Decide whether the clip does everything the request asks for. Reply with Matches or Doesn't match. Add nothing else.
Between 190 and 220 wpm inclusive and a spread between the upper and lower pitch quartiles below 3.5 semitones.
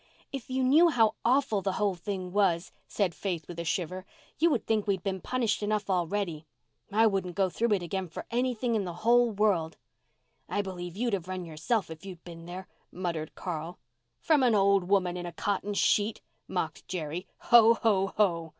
Doesn't match